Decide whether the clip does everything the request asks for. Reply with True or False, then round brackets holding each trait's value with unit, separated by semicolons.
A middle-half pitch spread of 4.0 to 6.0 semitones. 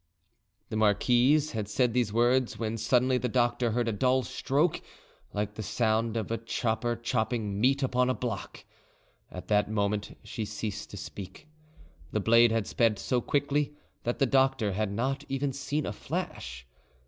False (3.3 semitones)